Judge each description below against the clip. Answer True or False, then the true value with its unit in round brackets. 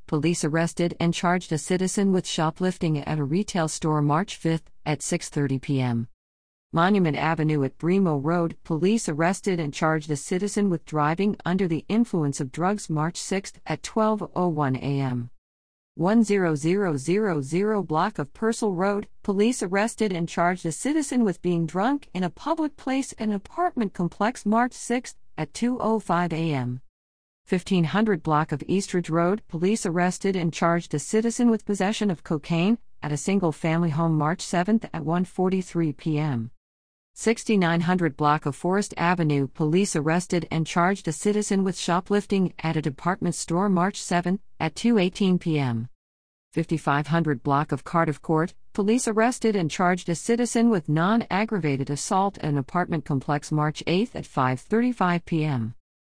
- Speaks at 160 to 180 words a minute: False (145 wpm)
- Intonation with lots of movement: False (4.6 semitones)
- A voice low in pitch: False (170 Hz)